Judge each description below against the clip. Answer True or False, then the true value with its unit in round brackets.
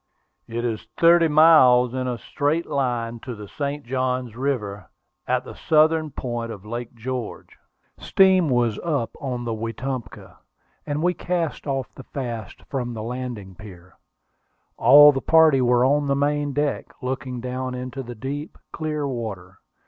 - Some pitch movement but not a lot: True (3.6 semitones)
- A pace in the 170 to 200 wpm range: False (155 wpm)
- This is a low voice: True (130 Hz)